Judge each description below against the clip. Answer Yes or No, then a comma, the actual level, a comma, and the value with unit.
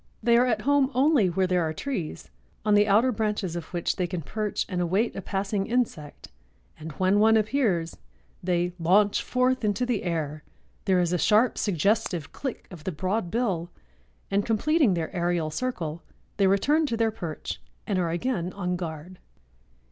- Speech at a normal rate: Yes, average, 175 wpm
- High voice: Yes, high, 195 Hz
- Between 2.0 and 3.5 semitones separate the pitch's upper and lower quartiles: No, average, 4.6 semitones